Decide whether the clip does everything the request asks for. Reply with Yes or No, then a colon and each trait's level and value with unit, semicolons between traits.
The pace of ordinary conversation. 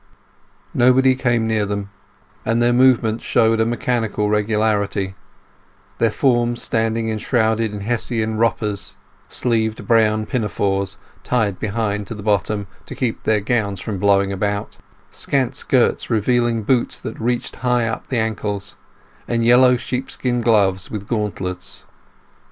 No: slow, 125 wpm